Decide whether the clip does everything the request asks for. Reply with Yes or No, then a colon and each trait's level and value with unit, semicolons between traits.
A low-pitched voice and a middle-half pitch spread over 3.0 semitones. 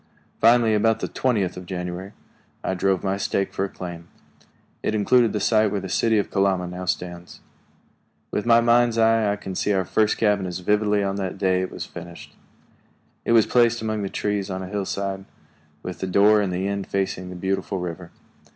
No: low, 100 Hz; narrow, 2.6 semitones